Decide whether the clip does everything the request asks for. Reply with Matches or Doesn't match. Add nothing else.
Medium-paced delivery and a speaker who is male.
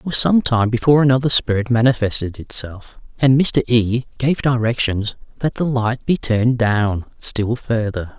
Matches